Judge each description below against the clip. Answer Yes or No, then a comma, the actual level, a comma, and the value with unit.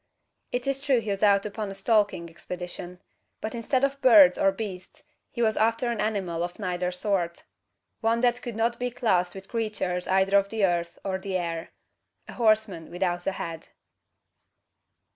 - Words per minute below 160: No, average, 175 wpm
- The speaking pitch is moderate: No, high, 200 Hz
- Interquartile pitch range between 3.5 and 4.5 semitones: Yes, average, 4.0 semitones